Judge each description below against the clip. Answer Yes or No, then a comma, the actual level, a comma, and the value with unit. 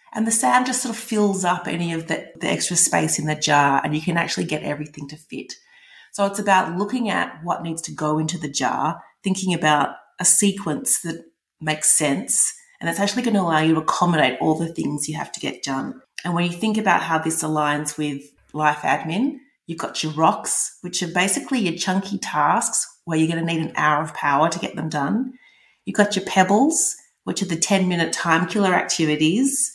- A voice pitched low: No, medium, 170 Hz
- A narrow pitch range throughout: No, average, 4.5 semitones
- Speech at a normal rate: No, fast, 215 wpm